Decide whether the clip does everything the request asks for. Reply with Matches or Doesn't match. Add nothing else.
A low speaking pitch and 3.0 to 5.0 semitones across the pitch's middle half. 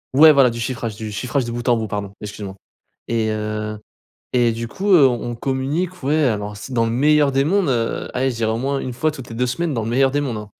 Matches